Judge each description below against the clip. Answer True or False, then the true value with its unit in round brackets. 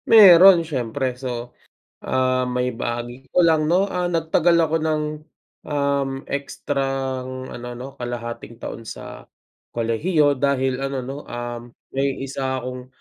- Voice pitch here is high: False (135 Hz)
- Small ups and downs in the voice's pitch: False (3.5 semitones)